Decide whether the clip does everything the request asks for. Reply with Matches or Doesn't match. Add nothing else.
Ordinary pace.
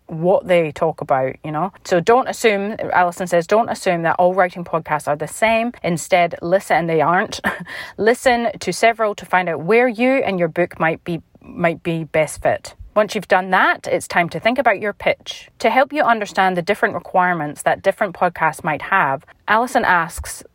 Matches